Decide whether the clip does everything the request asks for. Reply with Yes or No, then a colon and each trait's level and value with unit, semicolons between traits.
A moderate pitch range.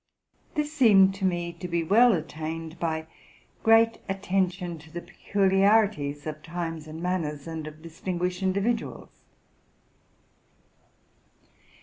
Yes: average, 3.4 semitones